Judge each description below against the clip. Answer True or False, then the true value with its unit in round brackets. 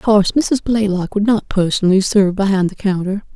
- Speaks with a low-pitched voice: False (200 Hz)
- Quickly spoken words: False (195 wpm)